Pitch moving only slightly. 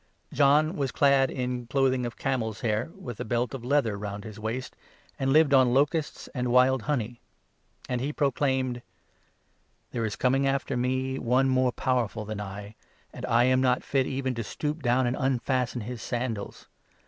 Yes: narrow, 2.2 semitones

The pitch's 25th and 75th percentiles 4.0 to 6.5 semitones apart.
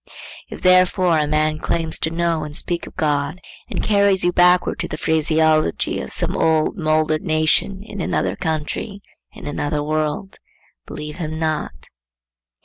No: narrow, 2.6 semitones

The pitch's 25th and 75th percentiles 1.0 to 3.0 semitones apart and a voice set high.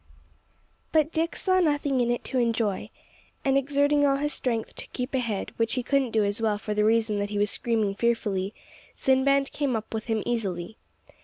No: average, 4.4 semitones; high, 235 Hz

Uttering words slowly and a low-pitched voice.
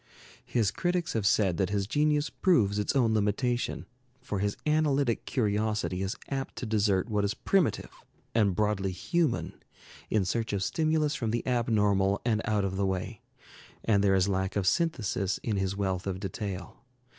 No: average, 170 wpm; low, 105 Hz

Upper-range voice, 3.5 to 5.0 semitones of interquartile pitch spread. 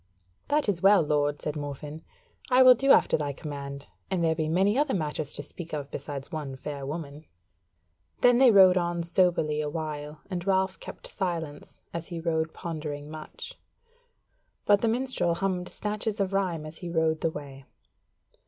No: medium, 165 Hz; average, 4.2 semitones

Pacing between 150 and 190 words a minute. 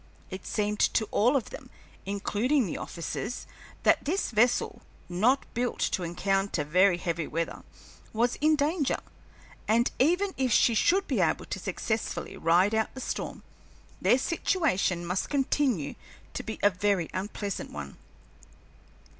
No: average, 140 wpm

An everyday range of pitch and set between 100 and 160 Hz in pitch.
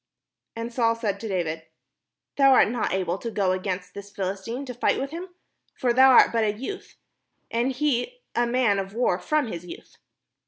No: average, 4.7 semitones; high, 230 Hz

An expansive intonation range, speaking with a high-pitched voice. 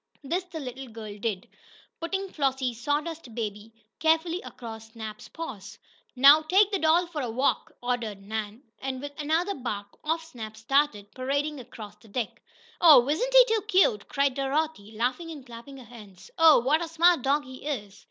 Yes: wide, 6.2 semitones; very high, 270 Hz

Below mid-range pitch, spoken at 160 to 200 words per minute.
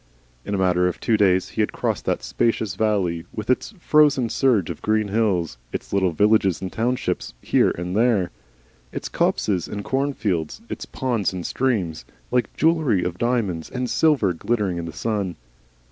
Yes: low, 105 Hz; average, 170 wpm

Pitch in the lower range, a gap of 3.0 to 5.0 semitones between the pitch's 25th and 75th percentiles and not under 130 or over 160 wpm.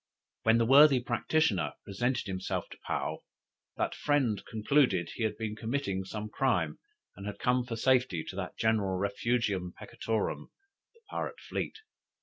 Yes: low, 110 Hz; average, 4.5 semitones; average, 145 wpm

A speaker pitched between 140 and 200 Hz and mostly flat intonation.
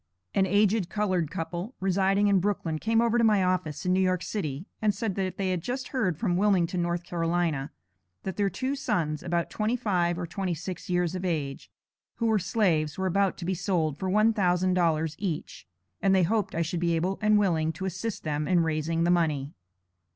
No: medium, 185 Hz; average, 3.2 semitones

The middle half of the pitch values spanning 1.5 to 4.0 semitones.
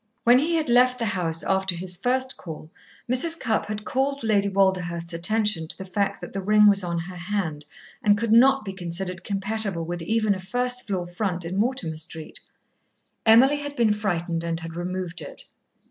No: average, 4.7 semitones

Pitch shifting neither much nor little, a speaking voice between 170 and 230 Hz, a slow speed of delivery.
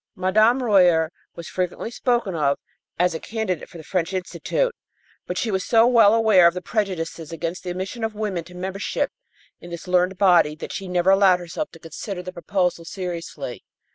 No: average, 3.2 semitones; medium, 185 Hz; average, 185 wpm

